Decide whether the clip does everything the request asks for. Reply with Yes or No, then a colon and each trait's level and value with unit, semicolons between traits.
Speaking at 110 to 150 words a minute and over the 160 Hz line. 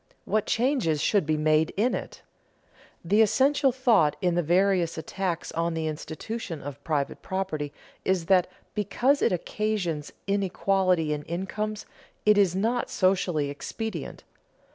Yes: slow, 135 wpm; medium, 185 Hz